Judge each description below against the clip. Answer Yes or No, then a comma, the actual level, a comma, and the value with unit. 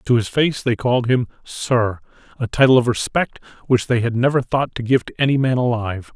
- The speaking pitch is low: Yes, low, 120 Hz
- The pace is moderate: No, fast, 215 wpm